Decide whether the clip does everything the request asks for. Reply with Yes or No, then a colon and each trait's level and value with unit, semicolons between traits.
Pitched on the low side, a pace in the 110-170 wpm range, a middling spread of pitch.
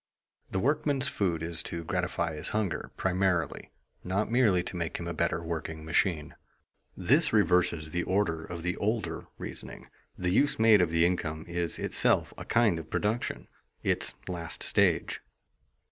Yes: very low, 90 Hz; average, 155 wpm; average, 3.7 semitones